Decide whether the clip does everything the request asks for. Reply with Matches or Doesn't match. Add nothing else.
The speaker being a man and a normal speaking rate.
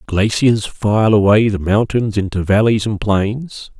Matches